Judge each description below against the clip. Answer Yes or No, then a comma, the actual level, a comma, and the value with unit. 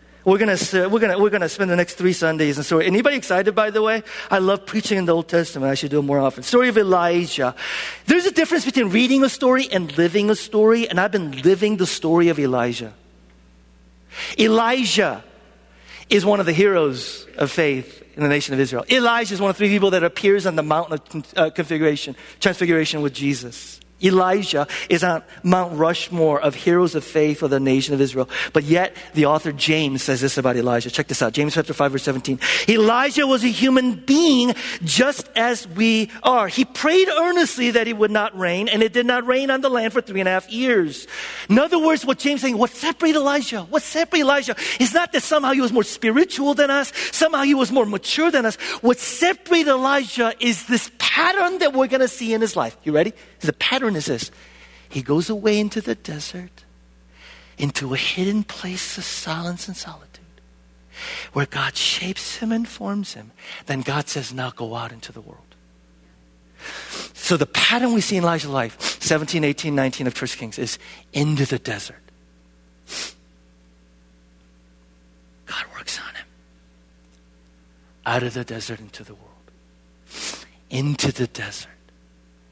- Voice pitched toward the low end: No, medium, 175 Hz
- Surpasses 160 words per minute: Yes, average, 185 wpm